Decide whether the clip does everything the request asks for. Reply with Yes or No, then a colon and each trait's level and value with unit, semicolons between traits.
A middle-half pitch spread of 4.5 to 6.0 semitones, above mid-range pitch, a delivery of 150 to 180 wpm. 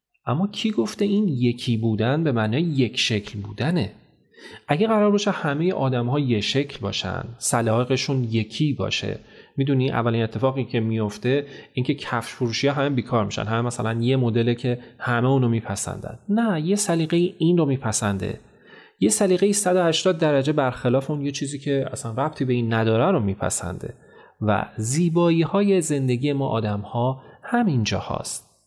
No: wide, 5.4 semitones; low, 130 Hz; fast, 155 wpm